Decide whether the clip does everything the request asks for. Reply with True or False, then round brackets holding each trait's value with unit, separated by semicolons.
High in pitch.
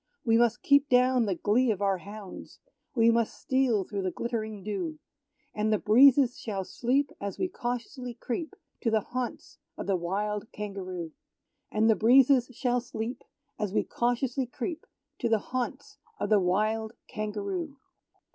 True (230 Hz)